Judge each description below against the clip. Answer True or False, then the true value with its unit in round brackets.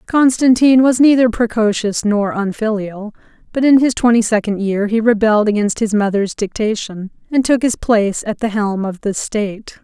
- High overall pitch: True (220 Hz)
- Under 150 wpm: False (170 wpm)